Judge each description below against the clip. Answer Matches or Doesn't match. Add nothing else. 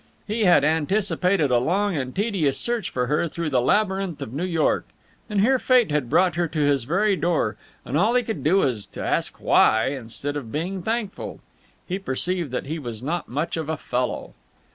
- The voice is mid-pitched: Matches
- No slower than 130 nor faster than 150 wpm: Doesn't match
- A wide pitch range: Matches